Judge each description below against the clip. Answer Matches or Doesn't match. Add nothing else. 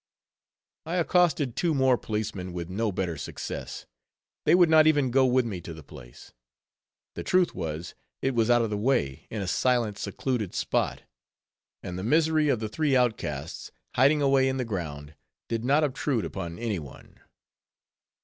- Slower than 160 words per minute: Doesn't match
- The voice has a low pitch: Matches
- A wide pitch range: Matches